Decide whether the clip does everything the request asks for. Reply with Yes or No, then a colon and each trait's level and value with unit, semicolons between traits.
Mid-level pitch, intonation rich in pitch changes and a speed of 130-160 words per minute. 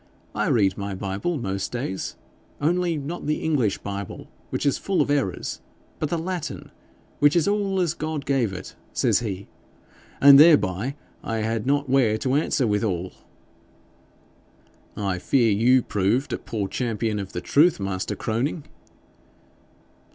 No: low, 120 Hz; wide, 6.7 semitones; average, 145 wpm